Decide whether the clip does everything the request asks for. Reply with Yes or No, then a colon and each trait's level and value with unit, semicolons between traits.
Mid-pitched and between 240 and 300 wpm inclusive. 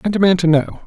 Yes: medium, 180 Hz; fast, 280 wpm